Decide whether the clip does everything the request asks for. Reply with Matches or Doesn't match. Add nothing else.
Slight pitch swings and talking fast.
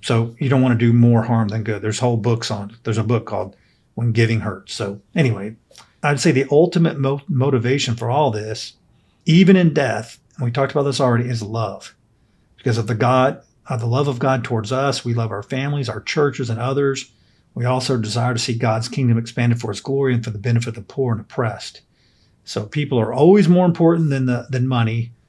Doesn't match